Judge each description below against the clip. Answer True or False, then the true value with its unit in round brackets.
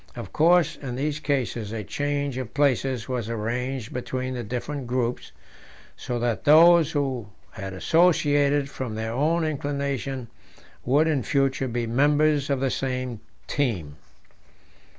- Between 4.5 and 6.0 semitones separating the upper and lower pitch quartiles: False (3.2 semitones)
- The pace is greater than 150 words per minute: False (135 wpm)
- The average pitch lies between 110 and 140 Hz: True (135 Hz)